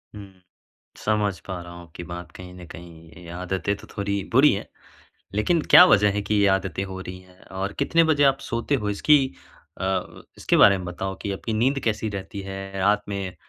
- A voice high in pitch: No, low, 100 Hz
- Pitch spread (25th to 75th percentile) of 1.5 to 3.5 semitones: Yes, narrow, 2.5 semitones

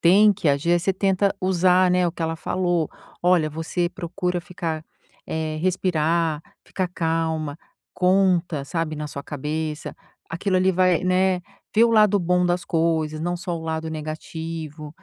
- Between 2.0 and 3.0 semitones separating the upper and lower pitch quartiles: Yes, narrow, 2.4 semitones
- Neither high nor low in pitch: Yes, medium, 170 Hz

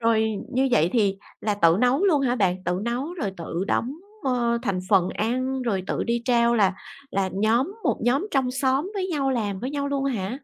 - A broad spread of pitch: No, average, 5.0 semitones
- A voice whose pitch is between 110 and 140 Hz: No, high, 235 Hz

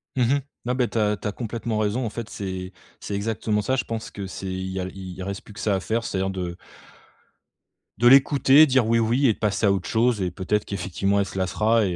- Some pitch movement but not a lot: Yes, average, 3.4 semitones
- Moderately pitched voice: No, low, 105 Hz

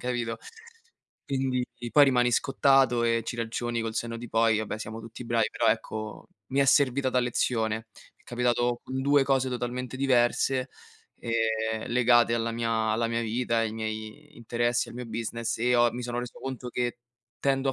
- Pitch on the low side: Yes, low, 120 Hz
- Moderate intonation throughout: No, narrow, 1.8 semitones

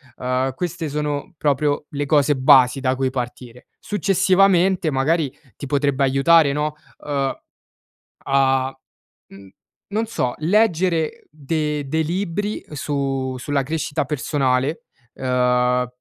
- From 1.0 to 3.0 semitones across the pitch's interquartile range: No, average, 3.6 semitones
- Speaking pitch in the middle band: Yes, medium, 145 Hz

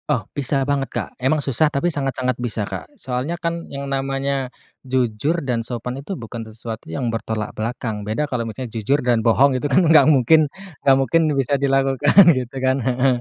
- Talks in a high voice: No, low, 130 Hz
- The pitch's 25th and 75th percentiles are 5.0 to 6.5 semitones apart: No, average, 3.0 semitones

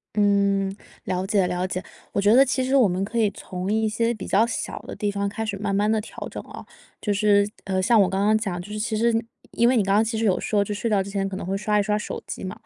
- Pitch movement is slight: Yes, narrow, 2.0 semitones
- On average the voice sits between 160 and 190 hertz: No, high, 205 Hz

